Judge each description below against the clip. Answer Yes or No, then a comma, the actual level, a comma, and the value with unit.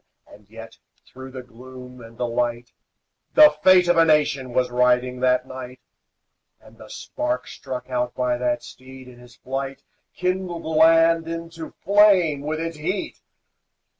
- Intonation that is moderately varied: Yes, average, 4.8 semitones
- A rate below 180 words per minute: Yes, average, 155 wpm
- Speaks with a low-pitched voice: Yes, low, 130 Hz